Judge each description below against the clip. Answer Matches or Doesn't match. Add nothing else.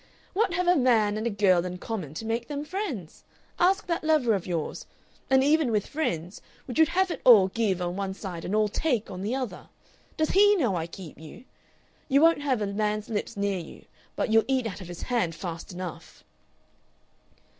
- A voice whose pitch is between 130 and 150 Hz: Doesn't match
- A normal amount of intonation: Doesn't match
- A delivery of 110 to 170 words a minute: Doesn't match